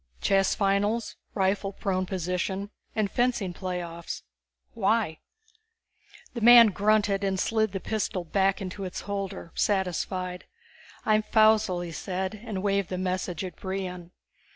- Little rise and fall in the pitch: Yes, narrow, 2.3 semitones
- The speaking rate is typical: No, slow, 130 wpm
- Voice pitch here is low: No, high, 195 Hz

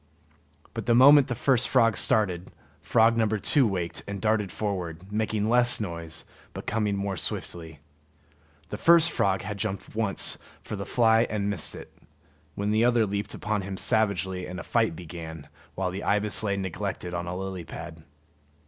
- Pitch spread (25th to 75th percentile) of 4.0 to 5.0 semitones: No, average, 3.3 semitones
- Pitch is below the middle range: Yes, low, 100 Hz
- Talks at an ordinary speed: Yes, average, 175 wpm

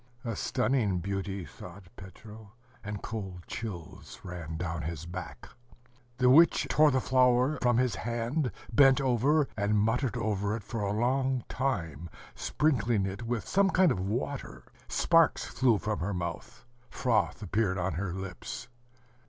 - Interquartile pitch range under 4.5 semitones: No, average, 5.1 semitones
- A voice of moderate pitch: No, low, 110 Hz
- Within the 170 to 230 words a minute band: No, average, 145 wpm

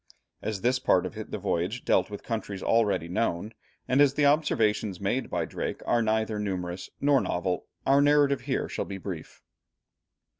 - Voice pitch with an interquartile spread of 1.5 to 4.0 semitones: No, wide, 5.4 semitones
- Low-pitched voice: Yes, low, 110 Hz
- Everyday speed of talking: Yes, average, 165 wpm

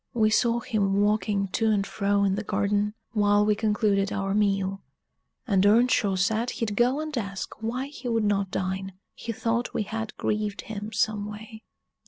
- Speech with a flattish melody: Yes, narrow, 2.0 semitones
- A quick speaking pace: No, average, 175 wpm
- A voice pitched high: Yes, high, 210 Hz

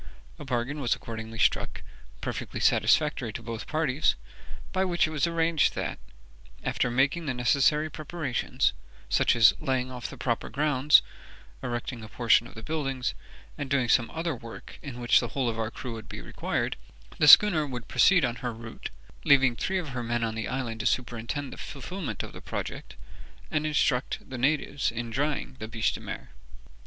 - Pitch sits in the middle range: No, low, 130 Hz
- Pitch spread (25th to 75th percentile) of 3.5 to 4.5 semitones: Yes, average, 4.1 semitones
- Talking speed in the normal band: Yes, average, 180 wpm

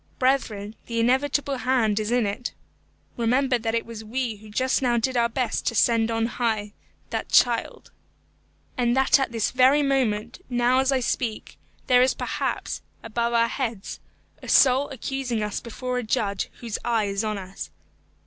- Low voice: No, high, 235 Hz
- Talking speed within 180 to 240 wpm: No, average, 170 wpm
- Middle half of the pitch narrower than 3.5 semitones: Yes, average, 2.8 semitones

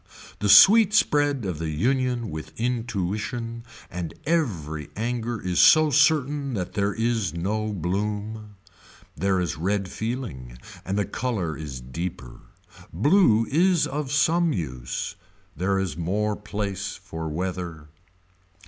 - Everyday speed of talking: No, slow, 125 wpm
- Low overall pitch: Yes, low, 105 Hz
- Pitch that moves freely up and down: Yes, wide, 6.3 semitones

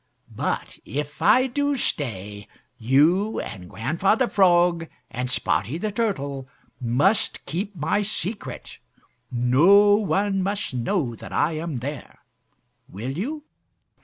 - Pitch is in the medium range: Yes, medium, 165 Hz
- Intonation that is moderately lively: No, wide, 8.1 semitones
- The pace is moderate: No, slow, 115 wpm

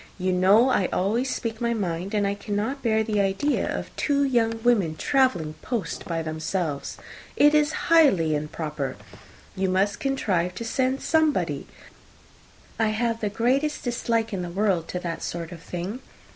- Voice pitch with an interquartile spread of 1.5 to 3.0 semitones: No, average, 5.3 semitones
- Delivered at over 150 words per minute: Yes, average, 160 wpm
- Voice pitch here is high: Yes, high, 210 Hz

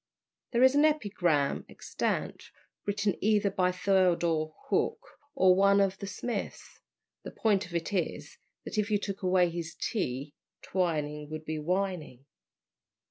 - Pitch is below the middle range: No, medium, 185 Hz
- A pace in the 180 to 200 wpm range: No, average, 140 wpm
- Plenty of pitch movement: No, average, 4.0 semitones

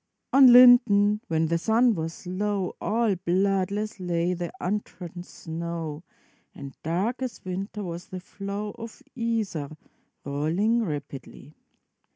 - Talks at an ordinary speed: No, slow, 125 wpm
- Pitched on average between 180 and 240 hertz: Yes, high, 190 Hz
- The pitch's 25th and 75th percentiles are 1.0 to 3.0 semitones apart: No, average, 4.1 semitones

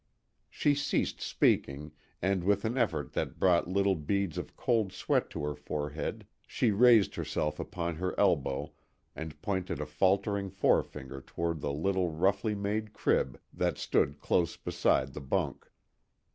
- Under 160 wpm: Yes, average, 145 wpm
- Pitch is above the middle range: No, very low, 90 Hz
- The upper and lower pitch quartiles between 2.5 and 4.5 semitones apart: No, average, 5.1 semitones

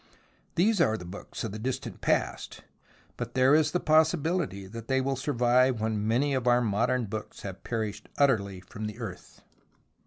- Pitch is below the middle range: Yes, low, 120 Hz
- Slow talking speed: No, average, 180 wpm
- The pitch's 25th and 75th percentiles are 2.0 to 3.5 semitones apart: No, average, 4.2 semitones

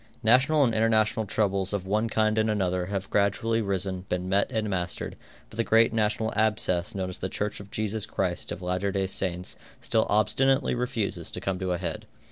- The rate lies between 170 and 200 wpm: Yes, average, 195 wpm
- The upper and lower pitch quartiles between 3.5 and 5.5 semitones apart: No, average, 2.7 semitones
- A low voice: Yes, low, 100 Hz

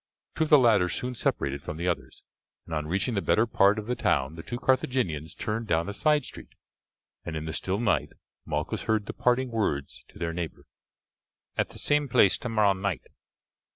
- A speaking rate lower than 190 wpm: No, average, 195 wpm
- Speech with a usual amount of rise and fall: No, wide, 6.7 semitones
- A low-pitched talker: Yes, low, 100 Hz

